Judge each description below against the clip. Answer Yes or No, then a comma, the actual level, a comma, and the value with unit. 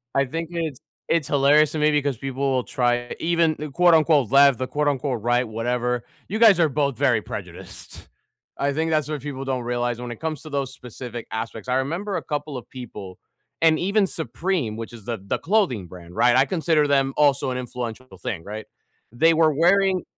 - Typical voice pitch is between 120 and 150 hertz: Yes, medium, 140 Hz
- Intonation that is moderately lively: Yes, average, 4.4 semitones